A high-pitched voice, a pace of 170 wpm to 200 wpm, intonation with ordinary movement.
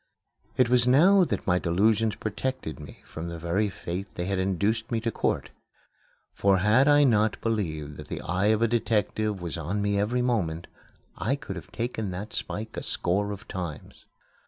No: low, 105 Hz; average, 180 wpm; average, 4.2 semitones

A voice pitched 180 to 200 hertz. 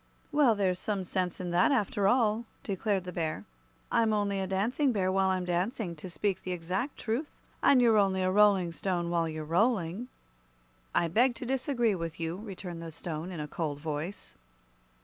Yes: high, 190 Hz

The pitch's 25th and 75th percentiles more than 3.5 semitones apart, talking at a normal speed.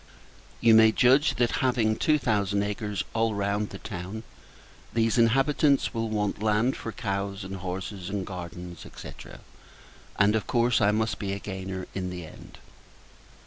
No: average, 2.8 semitones; average, 155 wpm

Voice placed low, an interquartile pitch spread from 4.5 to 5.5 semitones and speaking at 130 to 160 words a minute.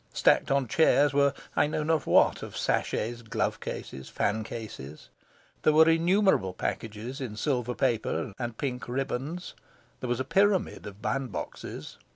Yes: low, 130 Hz; average, 5.1 semitones; average, 150 wpm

